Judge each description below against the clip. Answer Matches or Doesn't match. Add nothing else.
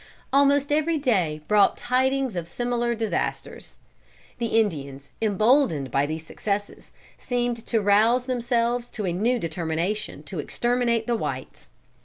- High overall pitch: Matches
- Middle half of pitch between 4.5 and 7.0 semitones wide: Matches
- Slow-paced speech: Matches